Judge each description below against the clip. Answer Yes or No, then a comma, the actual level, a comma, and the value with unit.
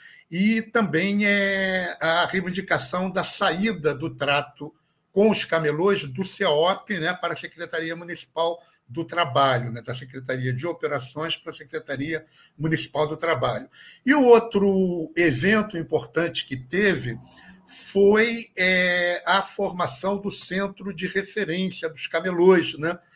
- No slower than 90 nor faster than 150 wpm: Yes, average, 130 wpm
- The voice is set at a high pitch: No, medium, 175 Hz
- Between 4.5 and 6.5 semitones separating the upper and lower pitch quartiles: No, average, 3.8 semitones